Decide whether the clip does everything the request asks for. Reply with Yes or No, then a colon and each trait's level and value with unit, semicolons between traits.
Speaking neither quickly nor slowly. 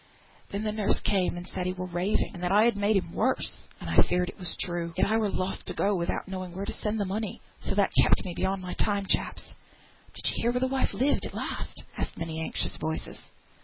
No: fast, 245 wpm